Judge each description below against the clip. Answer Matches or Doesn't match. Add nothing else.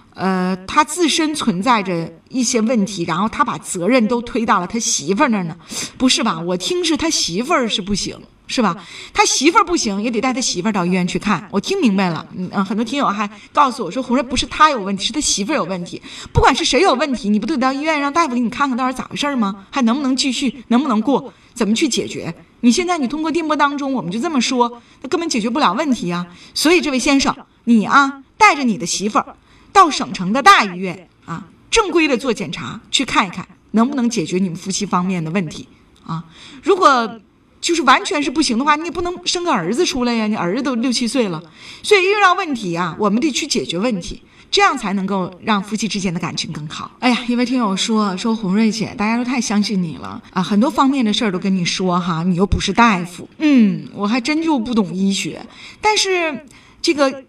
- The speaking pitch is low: Doesn't match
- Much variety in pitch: Matches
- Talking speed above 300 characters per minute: Matches